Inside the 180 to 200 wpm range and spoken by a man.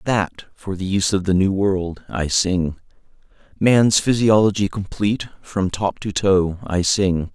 No: average, 155 wpm; male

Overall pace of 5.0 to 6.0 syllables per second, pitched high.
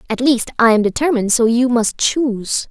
Yes: 5.4 syllables/s; high, 240 Hz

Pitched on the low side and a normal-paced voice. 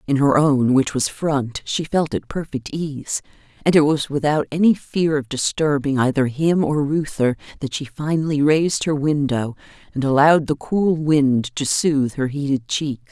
No: medium, 145 Hz; average, 180 wpm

